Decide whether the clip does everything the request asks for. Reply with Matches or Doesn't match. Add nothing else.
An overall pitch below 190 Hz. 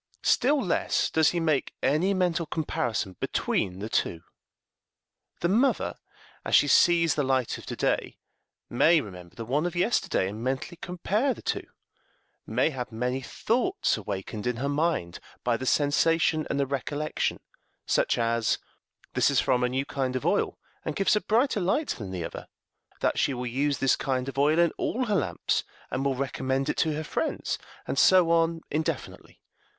Matches